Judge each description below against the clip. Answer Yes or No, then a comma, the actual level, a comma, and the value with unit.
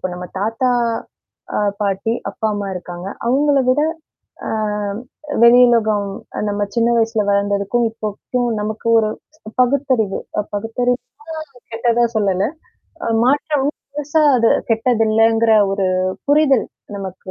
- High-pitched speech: Yes, high, 225 Hz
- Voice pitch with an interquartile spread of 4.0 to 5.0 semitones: No, average, 3.3 semitones